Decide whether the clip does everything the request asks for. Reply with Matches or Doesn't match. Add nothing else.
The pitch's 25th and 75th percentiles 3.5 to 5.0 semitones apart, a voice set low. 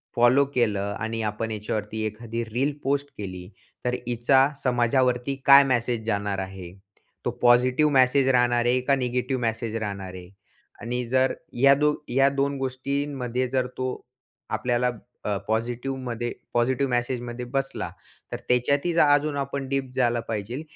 Doesn't match